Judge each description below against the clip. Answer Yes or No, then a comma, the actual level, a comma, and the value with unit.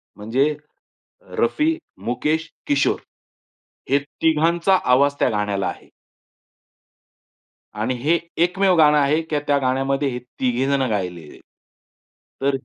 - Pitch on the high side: No, medium, 140 Hz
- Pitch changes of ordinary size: Yes, average, 4.4 semitones